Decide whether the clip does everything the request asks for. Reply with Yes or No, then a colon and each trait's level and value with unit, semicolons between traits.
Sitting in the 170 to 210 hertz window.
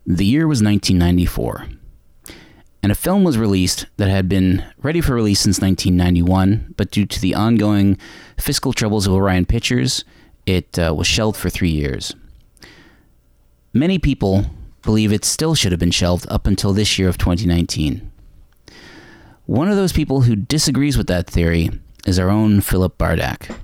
No: low, 100 Hz